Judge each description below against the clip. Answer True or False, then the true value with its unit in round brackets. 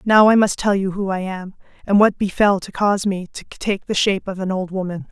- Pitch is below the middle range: False (195 Hz)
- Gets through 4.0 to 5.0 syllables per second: False (5.5 syllables/s)